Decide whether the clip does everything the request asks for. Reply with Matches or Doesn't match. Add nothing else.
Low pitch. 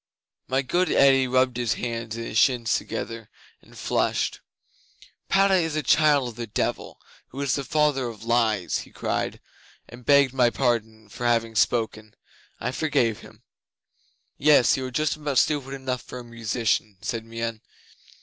Matches